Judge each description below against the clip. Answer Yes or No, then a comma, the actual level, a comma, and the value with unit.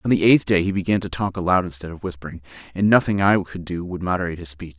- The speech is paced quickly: Yes, fast, 265 wpm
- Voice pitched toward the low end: Yes, very low, 90 Hz